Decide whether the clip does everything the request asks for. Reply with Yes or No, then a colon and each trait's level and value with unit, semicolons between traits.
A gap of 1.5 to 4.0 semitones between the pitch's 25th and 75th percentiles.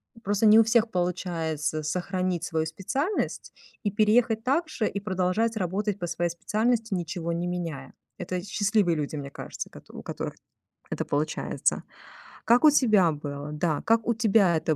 No: average, 5.0 semitones